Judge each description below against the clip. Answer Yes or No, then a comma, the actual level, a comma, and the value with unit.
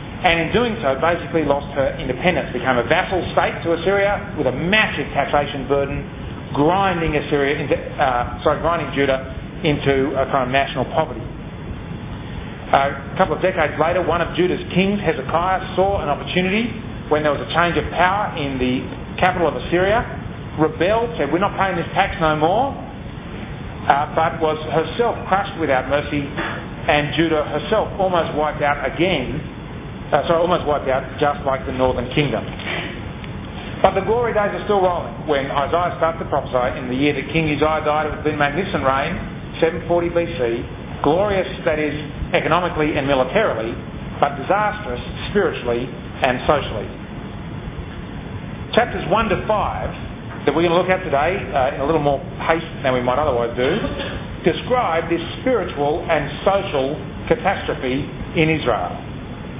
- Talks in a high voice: No, medium, 155 Hz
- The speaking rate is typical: Yes, average, 160 wpm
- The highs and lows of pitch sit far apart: No, average, 3.7 semitones